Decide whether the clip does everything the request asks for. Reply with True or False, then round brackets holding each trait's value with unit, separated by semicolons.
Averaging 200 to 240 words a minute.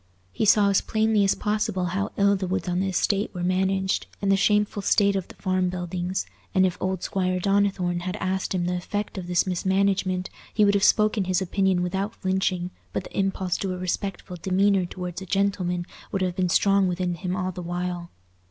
True (205 wpm)